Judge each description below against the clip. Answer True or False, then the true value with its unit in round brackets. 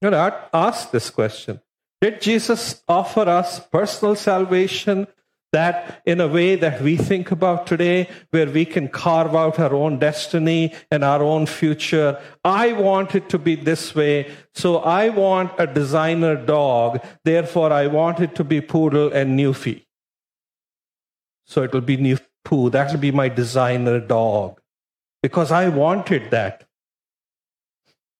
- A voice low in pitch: False (160 Hz)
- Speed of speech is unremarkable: True (145 wpm)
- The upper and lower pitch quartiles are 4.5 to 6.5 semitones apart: False (3.9 semitones)